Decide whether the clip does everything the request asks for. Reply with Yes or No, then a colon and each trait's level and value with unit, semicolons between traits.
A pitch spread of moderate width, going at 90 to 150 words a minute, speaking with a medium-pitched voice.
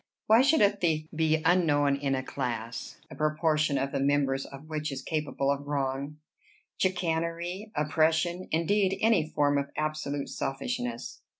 Yes: average, 3.3 semitones; average, 145 wpm; medium, 155 Hz